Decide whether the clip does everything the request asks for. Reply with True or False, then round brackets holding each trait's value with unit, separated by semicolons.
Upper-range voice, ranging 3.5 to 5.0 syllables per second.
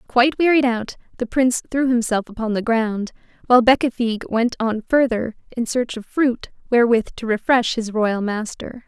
False (235 Hz; 5.2 syllables/s)